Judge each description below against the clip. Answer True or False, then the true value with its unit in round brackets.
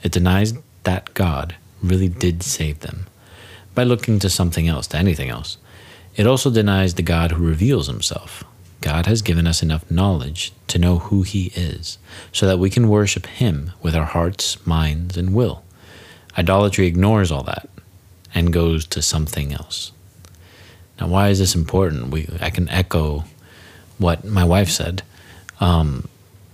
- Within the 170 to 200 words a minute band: False (160 wpm)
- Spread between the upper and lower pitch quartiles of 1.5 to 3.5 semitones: True (2.7 semitones)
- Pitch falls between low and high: False (90 Hz)